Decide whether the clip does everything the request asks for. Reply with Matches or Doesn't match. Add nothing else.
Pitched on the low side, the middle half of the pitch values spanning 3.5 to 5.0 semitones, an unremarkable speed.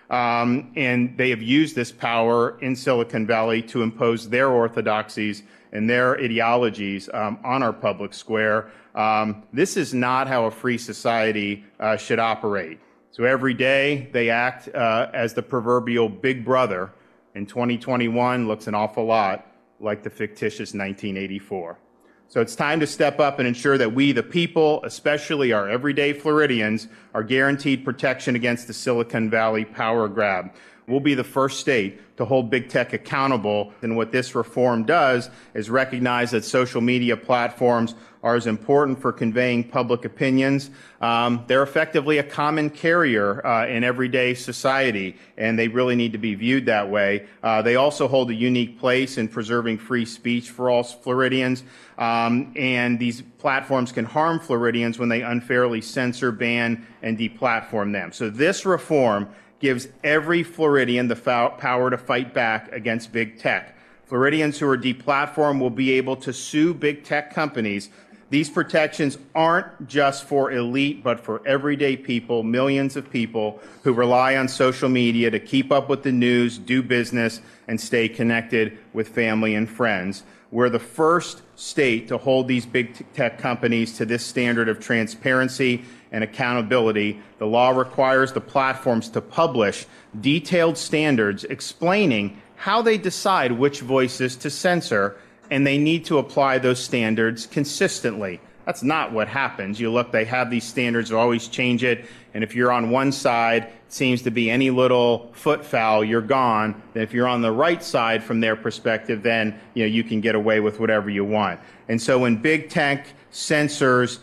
Doesn't match